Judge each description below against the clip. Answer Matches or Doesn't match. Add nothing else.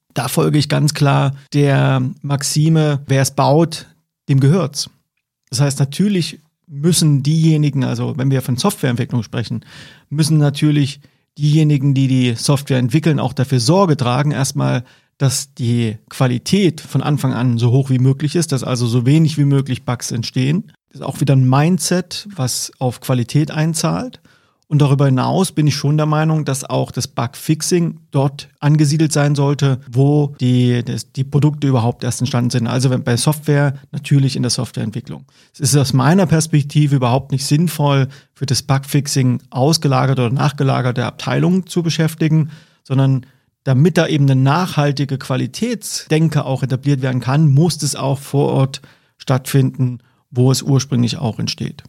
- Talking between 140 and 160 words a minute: Matches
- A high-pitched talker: Doesn't match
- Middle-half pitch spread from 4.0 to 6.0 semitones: Doesn't match